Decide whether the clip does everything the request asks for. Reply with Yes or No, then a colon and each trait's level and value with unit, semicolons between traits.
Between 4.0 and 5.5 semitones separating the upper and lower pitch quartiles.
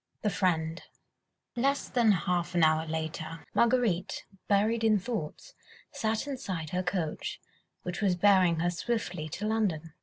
Yes: average, 5.0 semitones